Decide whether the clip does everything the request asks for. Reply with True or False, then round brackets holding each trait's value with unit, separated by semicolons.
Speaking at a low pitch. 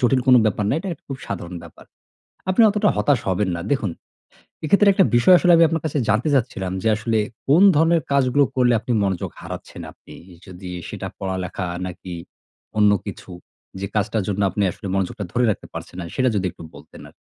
True (110 Hz)